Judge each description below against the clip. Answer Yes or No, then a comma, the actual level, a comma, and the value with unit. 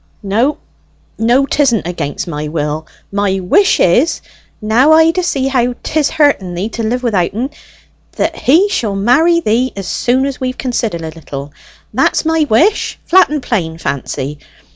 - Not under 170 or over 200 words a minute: No, average, 160 wpm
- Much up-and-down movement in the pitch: Yes, wide, 7.8 semitones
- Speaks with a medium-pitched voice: No, high, 235 Hz